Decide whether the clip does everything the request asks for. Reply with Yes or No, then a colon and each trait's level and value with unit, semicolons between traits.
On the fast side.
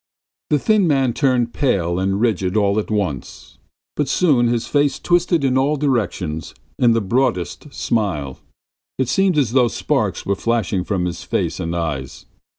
No: average, 160 wpm